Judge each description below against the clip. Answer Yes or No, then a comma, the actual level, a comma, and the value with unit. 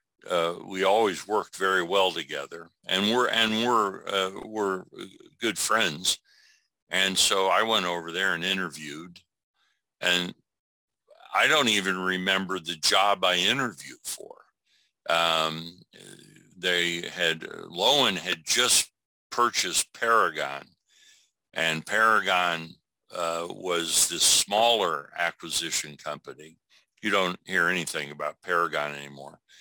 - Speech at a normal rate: No, slow, 115 wpm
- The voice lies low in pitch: Yes, very low, 90 Hz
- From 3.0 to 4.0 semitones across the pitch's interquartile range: No, narrow, 2.5 semitones